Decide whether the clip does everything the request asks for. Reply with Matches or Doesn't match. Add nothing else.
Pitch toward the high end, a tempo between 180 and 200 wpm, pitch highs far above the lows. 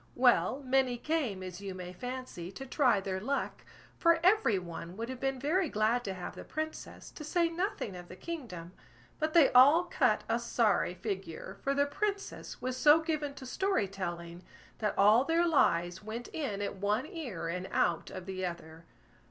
Matches